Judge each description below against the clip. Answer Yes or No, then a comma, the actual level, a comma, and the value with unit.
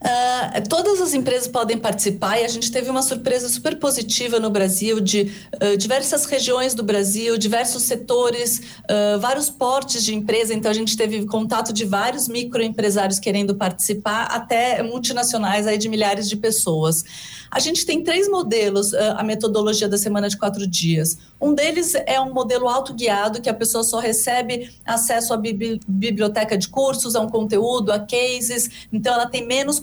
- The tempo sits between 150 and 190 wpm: Yes, average, 170 wpm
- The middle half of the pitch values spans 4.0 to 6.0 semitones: No, average, 3.0 semitones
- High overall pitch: Yes, high, 230 Hz